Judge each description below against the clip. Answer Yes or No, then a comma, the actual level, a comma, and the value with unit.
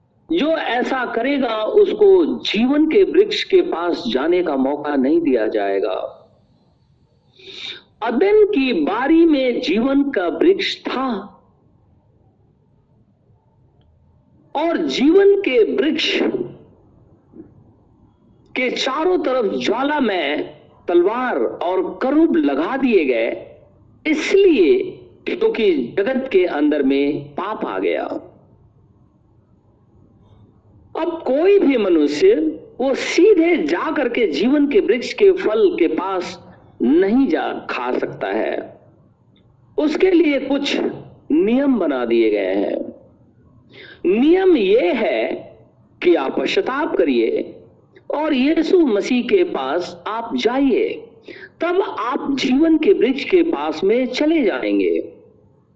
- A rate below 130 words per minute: Yes, slow, 110 wpm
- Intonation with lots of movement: Yes, wide, 6.4 semitones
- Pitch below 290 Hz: No, very high, 325 Hz